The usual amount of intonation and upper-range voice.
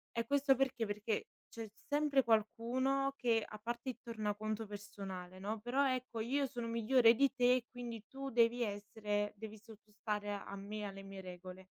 Yes: average, 3.2 semitones; high, 225 Hz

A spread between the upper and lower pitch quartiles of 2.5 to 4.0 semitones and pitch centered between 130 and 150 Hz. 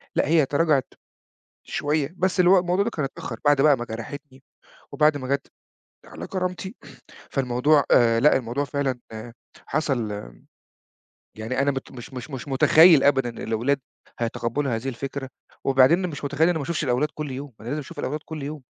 Yes: average, 3.1 semitones; medium, 140 Hz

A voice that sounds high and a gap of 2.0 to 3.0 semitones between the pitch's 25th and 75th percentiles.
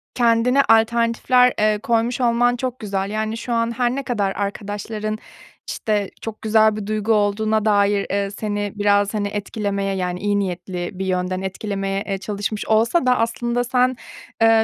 Yes: high, 215 Hz; narrow, 2.5 semitones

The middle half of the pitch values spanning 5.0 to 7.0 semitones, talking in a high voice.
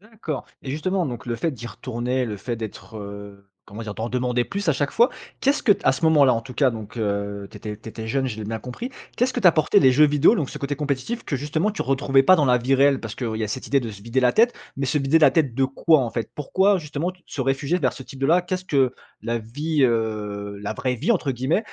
No: average, 5.3 semitones; low, 130 Hz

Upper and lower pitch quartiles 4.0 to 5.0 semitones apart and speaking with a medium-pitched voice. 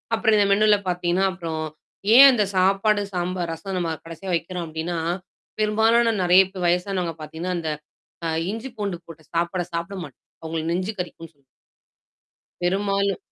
No: average, 3.2 semitones; medium, 180 Hz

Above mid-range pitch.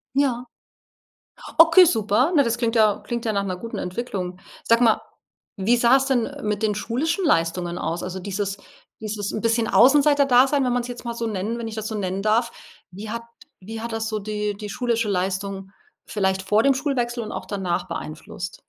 Yes: high, 220 Hz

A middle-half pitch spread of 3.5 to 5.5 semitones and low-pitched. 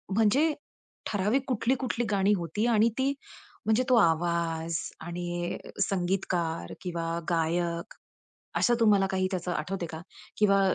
No: average, 4.3 semitones; medium, 185 Hz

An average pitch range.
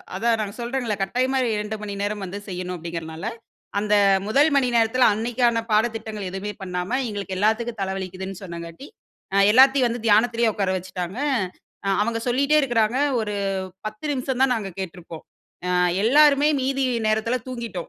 Yes: average, 4.2 semitones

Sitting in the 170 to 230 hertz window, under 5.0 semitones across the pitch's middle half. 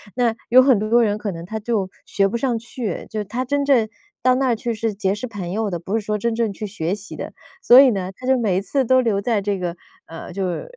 Yes: high, 220 Hz; average, 3.5 semitones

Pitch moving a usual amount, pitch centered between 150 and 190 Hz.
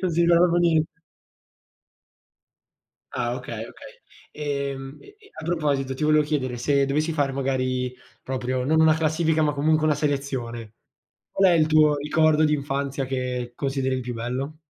No: average, 3.2 semitones; medium, 140 Hz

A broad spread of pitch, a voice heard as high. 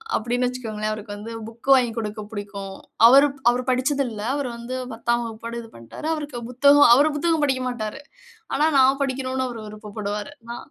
No: average, 3.8 semitones; high, 240 Hz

